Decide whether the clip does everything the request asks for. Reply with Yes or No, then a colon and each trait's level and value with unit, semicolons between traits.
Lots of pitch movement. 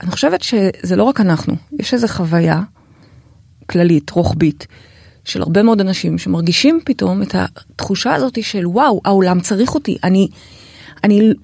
Yes: wide, 7.0 semitones